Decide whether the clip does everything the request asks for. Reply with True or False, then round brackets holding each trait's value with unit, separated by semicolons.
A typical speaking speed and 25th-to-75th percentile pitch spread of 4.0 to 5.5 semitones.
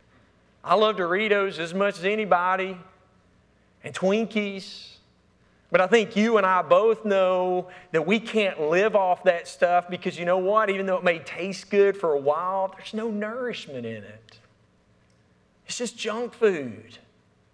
False (155 wpm; 3.0 semitones)